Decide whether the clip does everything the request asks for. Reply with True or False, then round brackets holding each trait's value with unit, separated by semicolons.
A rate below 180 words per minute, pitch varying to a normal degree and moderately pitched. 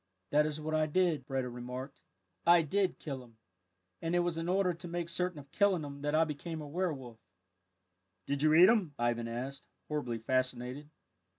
False (185 wpm; 4.7 semitones; 150 Hz)